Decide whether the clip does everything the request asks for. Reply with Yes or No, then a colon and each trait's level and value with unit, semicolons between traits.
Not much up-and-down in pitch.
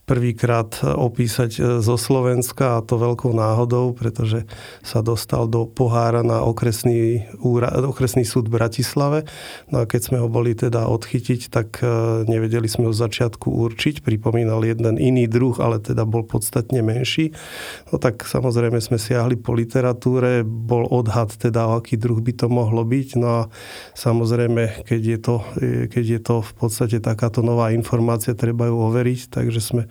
Yes: narrow, 1.2 semitones